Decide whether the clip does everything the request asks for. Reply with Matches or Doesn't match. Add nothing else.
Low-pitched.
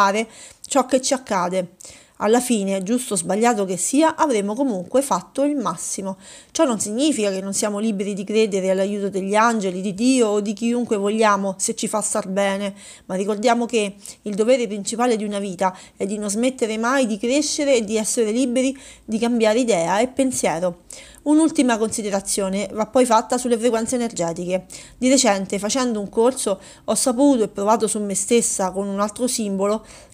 Doesn't match